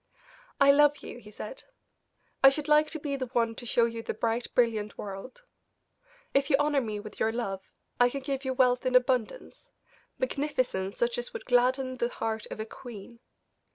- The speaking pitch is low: No, high, 245 Hz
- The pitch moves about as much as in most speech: Yes, average, 3.4 semitones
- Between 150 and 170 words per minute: No, average, 190 wpm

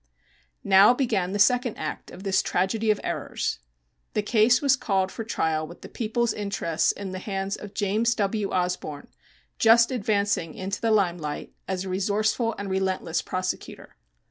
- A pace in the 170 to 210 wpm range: No, average, 160 wpm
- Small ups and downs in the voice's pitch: No, average, 3.0 semitones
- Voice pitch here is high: Yes, high, 200 Hz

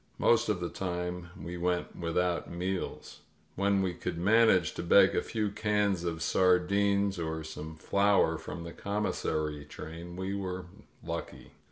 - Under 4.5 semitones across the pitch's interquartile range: Yes, average, 2.7 semitones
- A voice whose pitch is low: Yes, very low, 90 Hz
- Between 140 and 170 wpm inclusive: Yes, average, 150 wpm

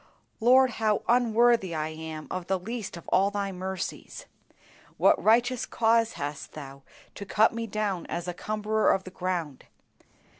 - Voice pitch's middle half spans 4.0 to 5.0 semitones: Yes, average, 4.4 semitones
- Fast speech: No, average, 155 wpm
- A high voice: Yes, high, 200 Hz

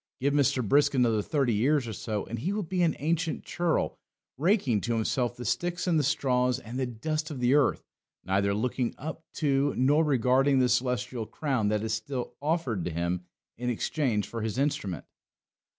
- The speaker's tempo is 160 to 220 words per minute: Yes, average, 185 wpm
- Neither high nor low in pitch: No, low, 130 Hz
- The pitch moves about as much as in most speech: Yes, average, 4.6 semitones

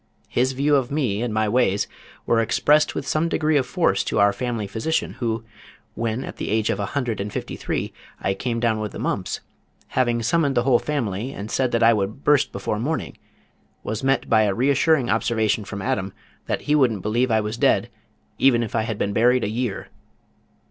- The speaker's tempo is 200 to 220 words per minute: Yes, fast, 205 wpm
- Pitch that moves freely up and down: No, average, 3.6 semitones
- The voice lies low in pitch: Yes, low, 115 Hz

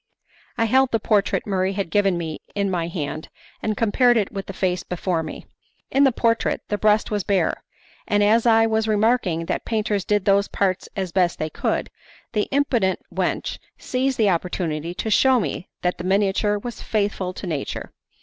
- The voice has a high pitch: Yes, high, 200 Hz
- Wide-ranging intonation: No, average, 3.4 semitones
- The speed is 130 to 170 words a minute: No, average, 185 wpm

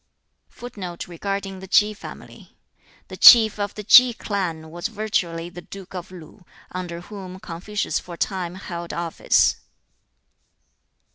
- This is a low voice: No, medium, 185 Hz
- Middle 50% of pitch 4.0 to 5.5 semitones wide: No, average, 3.0 semitones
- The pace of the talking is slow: Yes, slow, 120 wpm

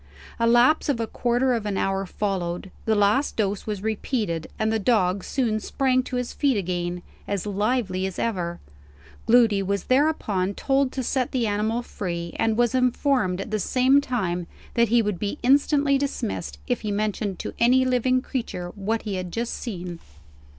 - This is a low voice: No, high, 220 Hz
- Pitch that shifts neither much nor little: Yes, average, 4.5 semitones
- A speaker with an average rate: Yes, average, 180 wpm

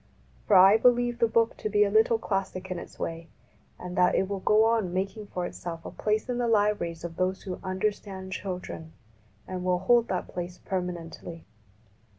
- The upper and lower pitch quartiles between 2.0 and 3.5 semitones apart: Yes, average, 3.1 semitones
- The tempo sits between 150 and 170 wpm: No, average, 185 wpm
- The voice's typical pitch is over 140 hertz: Yes, high, 190 Hz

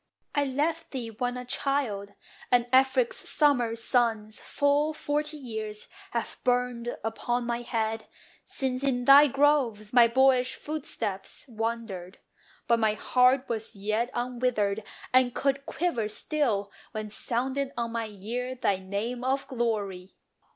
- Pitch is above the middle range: Yes, high, 240 Hz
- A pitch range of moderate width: Yes, average, 3.5 semitones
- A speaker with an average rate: No, slow, 130 wpm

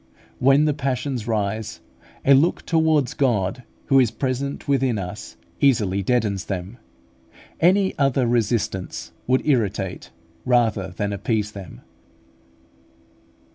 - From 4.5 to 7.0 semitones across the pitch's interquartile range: Yes, average, 5.0 semitones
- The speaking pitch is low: Yes, low, 120 Hz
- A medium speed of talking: No, slow, 110 wpm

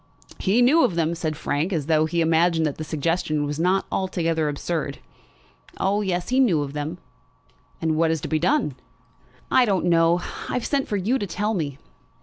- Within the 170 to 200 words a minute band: Yes, average, 190 wpm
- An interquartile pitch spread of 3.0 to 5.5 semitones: Yes, average, 3.8 semitones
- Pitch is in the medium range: Yes, medium, 165 Hz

